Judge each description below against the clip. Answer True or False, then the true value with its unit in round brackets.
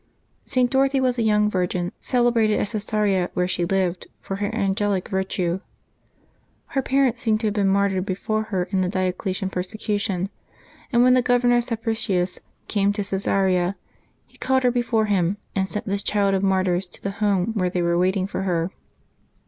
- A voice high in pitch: True (200 Hz)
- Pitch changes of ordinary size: True (3.0 semitones)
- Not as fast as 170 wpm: False (175 wpm)